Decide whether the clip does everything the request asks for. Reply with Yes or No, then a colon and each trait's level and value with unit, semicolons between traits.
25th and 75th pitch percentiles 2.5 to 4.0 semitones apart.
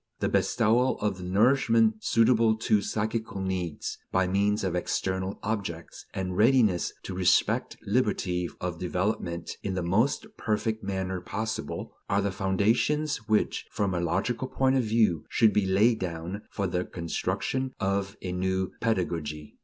Yes: average, 3.4 semitones